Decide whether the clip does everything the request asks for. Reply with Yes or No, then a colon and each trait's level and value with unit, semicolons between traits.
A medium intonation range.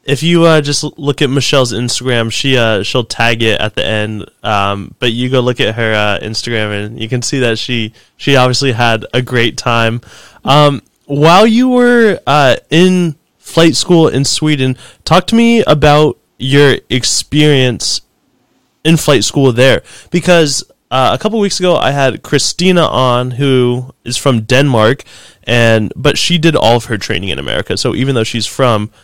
Yes: average, 4.6 semitones